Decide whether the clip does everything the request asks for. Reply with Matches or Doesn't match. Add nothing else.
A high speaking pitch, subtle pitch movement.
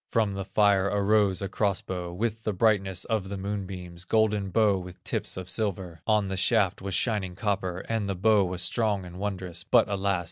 Doesn't match